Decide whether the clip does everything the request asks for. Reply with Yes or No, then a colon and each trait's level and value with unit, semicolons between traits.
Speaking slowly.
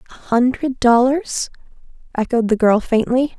Yes: slow, 125 wpm